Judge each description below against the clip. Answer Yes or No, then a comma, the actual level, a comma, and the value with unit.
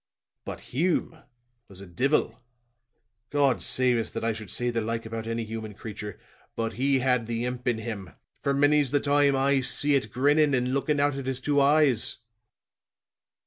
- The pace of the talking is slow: No, average, 180 wpm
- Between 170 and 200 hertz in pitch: No, low, 125 Hz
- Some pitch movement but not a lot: Yes, average, 3.7 semitones